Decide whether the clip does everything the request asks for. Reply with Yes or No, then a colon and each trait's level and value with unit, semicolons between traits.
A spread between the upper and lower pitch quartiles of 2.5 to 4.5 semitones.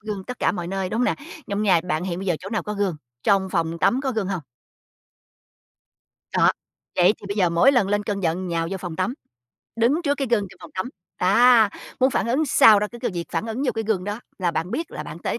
Yes: average, 4.2 semitones